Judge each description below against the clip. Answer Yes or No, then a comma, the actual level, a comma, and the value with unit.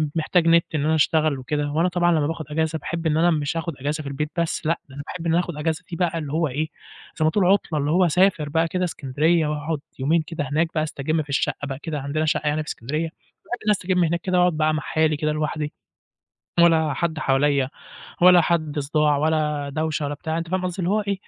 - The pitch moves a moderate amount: No, narrow, 2.2 semitones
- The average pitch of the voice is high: No, medium, 155 Hz